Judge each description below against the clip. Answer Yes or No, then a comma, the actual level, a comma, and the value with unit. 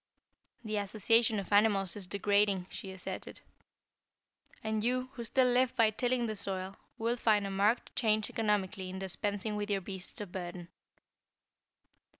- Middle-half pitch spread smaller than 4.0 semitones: Yes, narrow, 2.6 semitones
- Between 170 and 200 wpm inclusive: No, average, 150 wpm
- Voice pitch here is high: Yes, high, 210 Hz